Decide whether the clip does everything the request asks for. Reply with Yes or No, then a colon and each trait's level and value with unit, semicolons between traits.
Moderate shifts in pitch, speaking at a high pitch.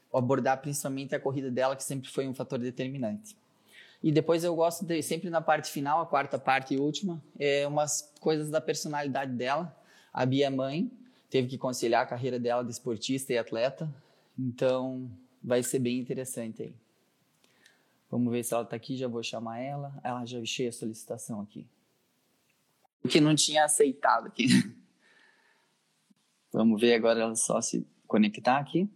No: average, 3.8 semitones; low, 135 Hz